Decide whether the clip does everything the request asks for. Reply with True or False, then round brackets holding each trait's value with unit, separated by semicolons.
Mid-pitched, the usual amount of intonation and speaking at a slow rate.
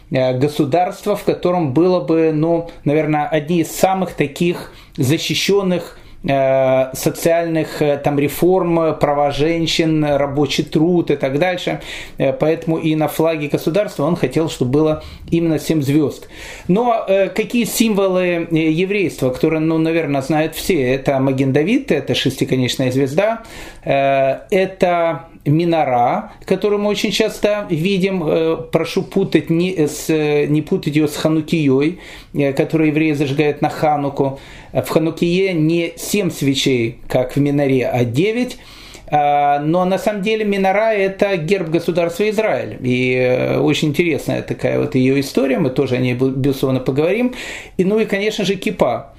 False (160 Hz; 4.1 semitones; 140 wpm)